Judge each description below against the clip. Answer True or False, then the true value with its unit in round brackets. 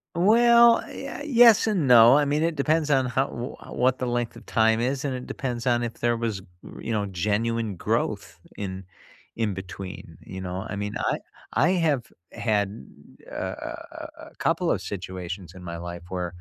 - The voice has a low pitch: True (115 Hz)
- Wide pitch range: True (6.5 semitones)